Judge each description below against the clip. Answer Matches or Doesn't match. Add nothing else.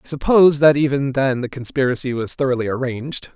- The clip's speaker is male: Matches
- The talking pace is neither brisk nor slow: Matches